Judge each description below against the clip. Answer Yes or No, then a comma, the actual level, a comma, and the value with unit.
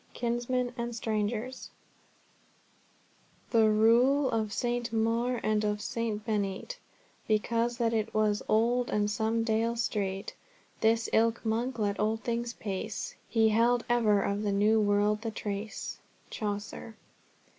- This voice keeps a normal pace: No, slow, 130 wpm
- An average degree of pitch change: No, narrow, 2.0 semitones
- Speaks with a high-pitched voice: Yes, high, 225 Hz